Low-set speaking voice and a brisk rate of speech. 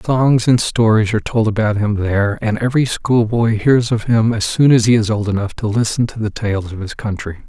Yes: low, 110 Hz; fast, 240 wpm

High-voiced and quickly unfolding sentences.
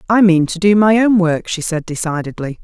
No: medium, 180 Hz; fast, 230 wpm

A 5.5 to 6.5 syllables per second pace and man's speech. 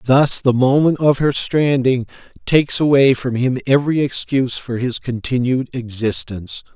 No: 4.8 syllables/s; male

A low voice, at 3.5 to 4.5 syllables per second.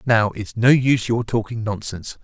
No: low, 115 Hz; 5.2 syllables/s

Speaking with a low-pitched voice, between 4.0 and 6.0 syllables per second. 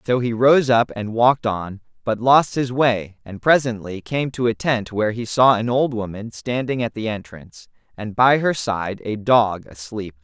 Yes: low, 115 Hz; 4.5 syllables/s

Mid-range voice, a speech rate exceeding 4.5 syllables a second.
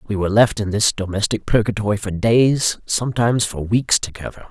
No: low, 105 Hz; 5.4 syllables/s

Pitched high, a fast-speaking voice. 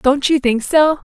Yes: very high, 280 Hz; fast, 215 wpm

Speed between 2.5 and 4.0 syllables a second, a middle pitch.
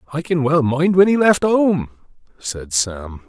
Yes: 3.8 syllables/s; medium, 150 Hz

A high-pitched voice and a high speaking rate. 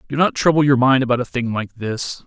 No: low, 130 Hz; fast, 265 wpm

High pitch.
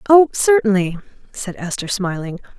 Yes: high, 215 Hz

